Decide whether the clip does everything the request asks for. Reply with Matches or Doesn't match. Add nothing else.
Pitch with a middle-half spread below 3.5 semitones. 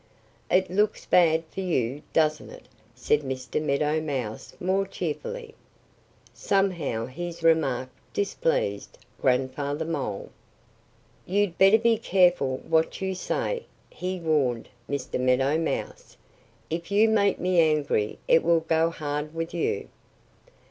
Doesn't match